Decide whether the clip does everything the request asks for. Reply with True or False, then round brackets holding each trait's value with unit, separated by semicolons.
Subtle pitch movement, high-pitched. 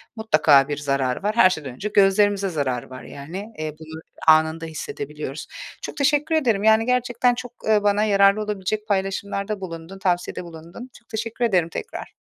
False (5.4 semitones; 195 Hz)